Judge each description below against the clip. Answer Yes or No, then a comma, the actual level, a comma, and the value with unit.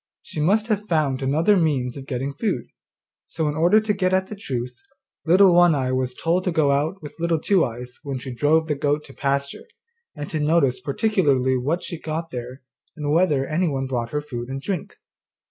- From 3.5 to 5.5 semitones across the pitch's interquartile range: Yes, average, 4.4 semitones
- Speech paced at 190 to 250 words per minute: Yes, average, 200 wpm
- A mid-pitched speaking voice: Yes, medium, 150 Hz